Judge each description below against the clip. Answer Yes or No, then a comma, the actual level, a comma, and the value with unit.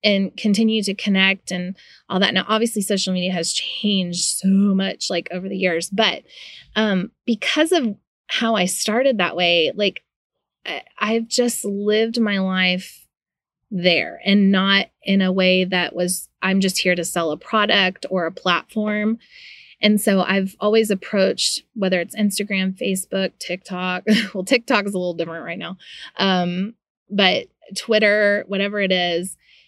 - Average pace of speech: Yes, average, 155 wpm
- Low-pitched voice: No, high, 195 Hz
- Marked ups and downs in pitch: No, narrow, 2.5 semitones